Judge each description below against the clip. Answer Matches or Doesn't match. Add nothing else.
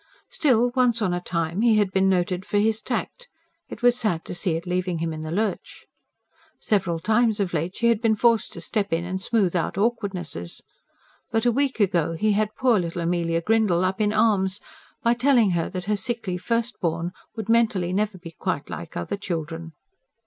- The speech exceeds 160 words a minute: Matches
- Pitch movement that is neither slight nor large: Matches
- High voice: Matches